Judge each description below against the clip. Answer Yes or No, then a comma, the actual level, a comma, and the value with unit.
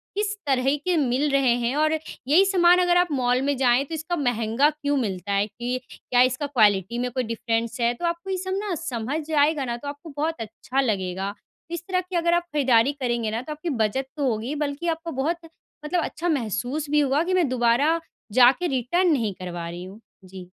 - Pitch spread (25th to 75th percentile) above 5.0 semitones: Yes, wide, 5.5 semitones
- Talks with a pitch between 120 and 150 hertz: No, very high, 275 Hz